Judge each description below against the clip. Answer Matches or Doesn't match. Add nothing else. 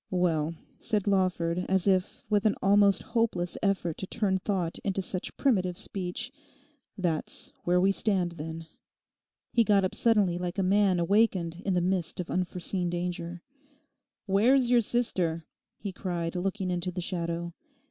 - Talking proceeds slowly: Doesn't match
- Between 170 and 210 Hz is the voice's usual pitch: Matches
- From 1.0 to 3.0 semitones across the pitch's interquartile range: Matches